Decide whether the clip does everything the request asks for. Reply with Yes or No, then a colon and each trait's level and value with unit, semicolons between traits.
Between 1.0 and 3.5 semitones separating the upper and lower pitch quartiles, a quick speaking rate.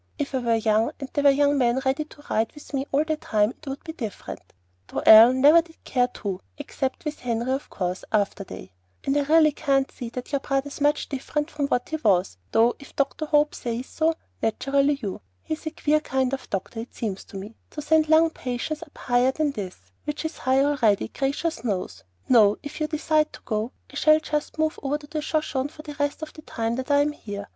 No: average, 4.3 semitones; fast, 225 wpm